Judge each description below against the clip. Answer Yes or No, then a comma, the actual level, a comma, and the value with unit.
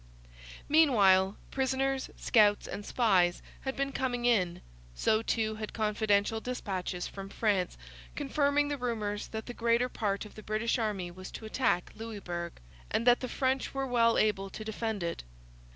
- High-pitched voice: Yes, high, 220 Hz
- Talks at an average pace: Yes, average, 155 wpm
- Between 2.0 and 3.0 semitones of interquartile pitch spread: No, average, 3.8 semitones